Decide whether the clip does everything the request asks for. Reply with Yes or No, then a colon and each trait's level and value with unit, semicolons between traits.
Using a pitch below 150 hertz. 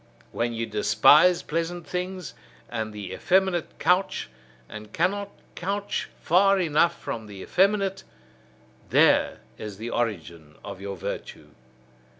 No: medium, 160 Hz